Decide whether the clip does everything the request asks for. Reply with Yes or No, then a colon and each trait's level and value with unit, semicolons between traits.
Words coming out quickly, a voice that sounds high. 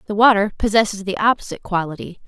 No: average, 160 wpm; high, 205 Hz